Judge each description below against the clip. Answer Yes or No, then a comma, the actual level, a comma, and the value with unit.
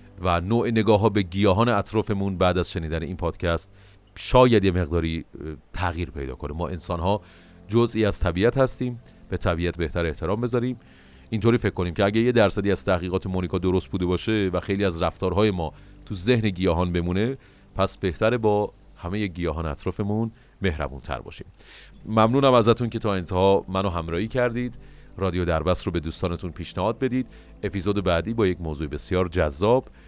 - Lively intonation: No, average, 3.9 semitones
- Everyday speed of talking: No, fast, 165 wpm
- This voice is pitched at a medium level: No, very low, 95 Hz